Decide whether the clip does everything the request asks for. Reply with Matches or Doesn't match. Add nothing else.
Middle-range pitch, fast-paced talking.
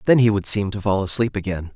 Doesn't match